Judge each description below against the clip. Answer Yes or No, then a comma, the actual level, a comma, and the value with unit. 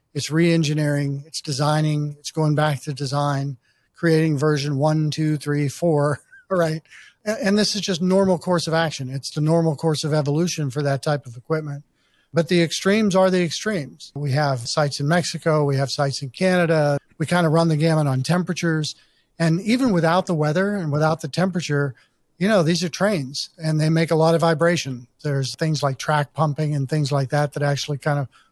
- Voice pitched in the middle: Yes, medium, 155 Hz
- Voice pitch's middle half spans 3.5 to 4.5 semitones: No, average, 2.7 semitones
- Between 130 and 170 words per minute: No, average, 195 wpm